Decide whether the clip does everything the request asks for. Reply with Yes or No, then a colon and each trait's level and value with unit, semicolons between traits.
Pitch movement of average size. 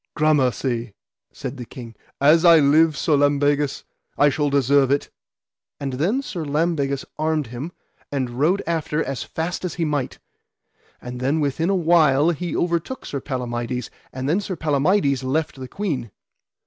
Yes: average, 3.5 semitones